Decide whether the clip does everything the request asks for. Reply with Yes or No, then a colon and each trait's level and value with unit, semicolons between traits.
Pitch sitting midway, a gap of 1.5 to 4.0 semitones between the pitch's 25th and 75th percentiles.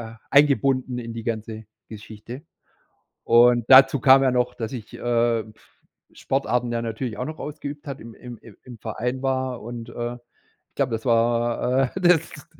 No: low, 120 Hz; narrow, 2.4 semitones